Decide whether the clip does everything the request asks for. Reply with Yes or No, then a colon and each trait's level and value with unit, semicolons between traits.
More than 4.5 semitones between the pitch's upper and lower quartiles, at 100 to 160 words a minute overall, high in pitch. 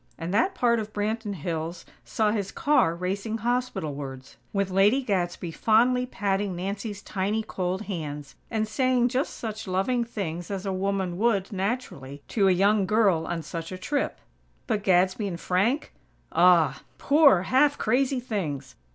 No: average, 4.2 semitones; average, 150 wpm; high, 200 Hz